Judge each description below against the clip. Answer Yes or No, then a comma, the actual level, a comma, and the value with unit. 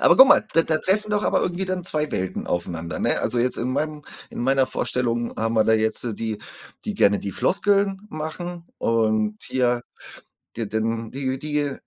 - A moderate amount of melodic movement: No, wide, 6.6 semitones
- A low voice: Yes, low, 130 Hz